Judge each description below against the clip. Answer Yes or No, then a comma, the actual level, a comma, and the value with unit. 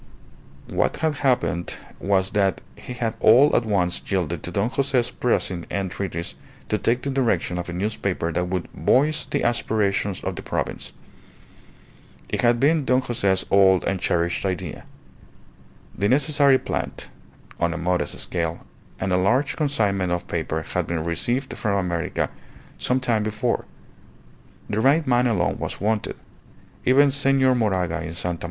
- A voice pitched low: Yes, low, 100 Hz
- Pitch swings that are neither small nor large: No, wide, 6.1 semitones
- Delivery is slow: No, average, 155 wpm